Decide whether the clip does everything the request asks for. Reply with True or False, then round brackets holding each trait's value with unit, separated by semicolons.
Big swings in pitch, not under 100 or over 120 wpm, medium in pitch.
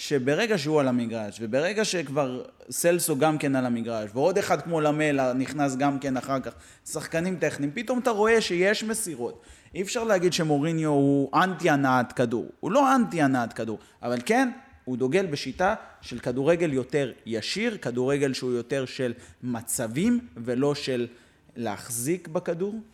False (6.1 semitones; 150 wpm; 145 Hz)